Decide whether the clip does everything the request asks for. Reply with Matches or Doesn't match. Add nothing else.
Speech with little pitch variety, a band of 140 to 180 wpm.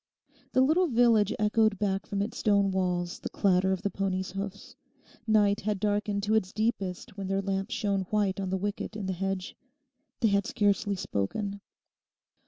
Matches